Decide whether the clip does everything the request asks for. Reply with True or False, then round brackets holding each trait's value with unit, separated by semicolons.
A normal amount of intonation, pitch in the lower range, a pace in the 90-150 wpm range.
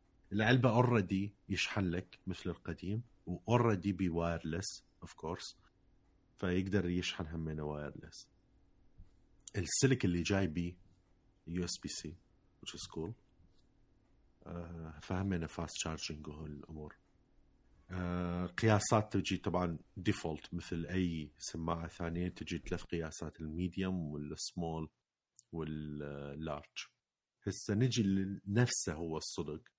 True (3.2 semitones; 90 Hz; 100 wpm)